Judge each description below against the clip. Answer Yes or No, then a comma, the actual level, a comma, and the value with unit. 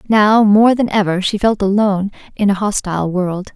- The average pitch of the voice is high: Yes, high, 200 Hz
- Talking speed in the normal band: Yes, average, 185 wpm